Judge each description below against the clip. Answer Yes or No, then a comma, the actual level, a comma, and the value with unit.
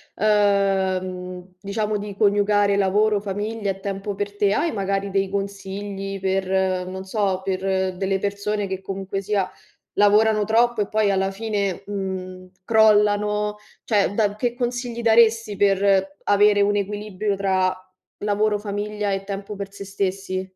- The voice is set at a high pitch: Yes, high, 200 Hz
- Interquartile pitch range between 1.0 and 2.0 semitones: Yes, narrow, 1.4 semitones